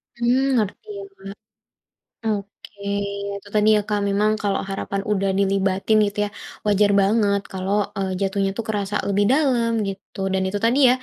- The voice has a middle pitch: No, high, 205 Hz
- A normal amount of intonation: No, narrow, 1.6 semitones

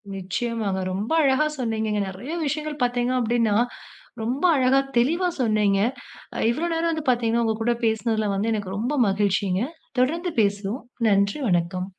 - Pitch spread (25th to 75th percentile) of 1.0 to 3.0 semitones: No, average, 4.2 semitones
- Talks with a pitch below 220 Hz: No, high, 230 Hz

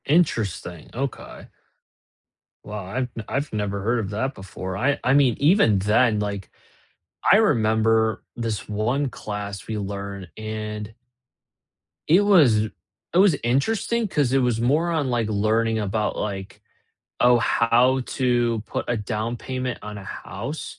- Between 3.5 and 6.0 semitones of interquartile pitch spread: Yes, average, 4.0 semitones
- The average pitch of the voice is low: Yes, low, 115 Hz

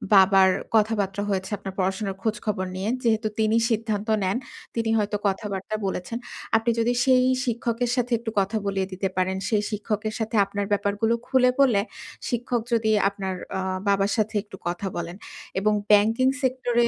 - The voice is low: No, high, 210 Hz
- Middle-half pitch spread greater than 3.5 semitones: No, average, 2.9 semitones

